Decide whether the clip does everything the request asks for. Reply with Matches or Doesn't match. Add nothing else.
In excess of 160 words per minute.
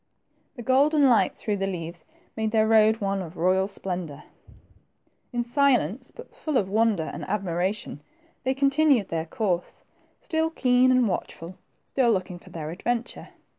Doesn't match